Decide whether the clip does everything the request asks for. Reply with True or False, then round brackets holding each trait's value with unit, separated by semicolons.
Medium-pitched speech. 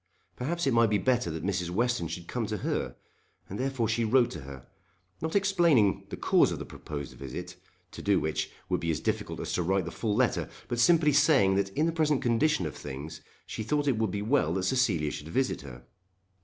False (110 Hz)